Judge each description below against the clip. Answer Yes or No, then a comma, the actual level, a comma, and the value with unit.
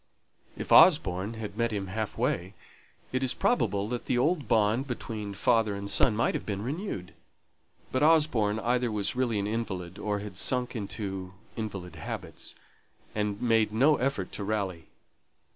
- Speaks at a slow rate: No, average, 160 wpm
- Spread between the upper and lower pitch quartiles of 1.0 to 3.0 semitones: No, average, 3.6 semitones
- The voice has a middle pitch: No, low, 110 Hz